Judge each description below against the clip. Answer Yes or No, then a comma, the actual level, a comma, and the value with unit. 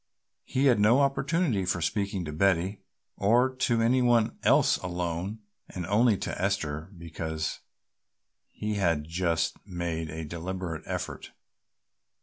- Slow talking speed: Yes, slow, 130 wpm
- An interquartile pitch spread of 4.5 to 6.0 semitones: Yes, average, 5.3 semitones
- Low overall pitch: Yes, very low, 95 Hz